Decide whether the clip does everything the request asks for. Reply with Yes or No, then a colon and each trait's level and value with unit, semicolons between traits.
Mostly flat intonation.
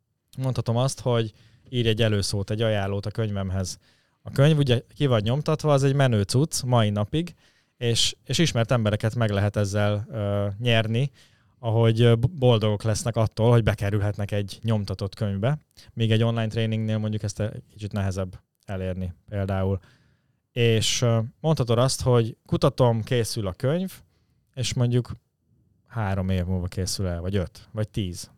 No: average, 3.1 semitones